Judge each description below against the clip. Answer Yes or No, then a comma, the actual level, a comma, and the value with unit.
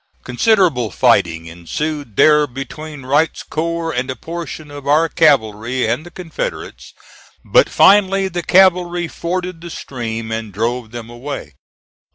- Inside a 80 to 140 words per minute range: Yes, slow, 135 wpm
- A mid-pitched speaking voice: Yes, medium, 150 Hz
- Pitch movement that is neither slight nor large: No, wide, 6.3 semitones